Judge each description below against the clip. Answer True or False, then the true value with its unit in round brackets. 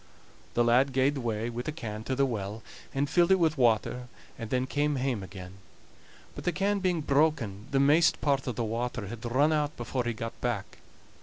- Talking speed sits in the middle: False (210 wpm)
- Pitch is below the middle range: True (125 Hz)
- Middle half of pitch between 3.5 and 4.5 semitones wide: True (4.2 semitones)